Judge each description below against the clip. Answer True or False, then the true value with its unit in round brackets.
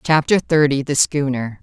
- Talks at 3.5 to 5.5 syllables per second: True (4.6 syllables/s)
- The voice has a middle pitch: True (145 Hz)